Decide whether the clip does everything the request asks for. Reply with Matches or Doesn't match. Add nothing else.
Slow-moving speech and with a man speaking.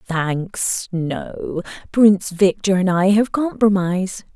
Doesn't match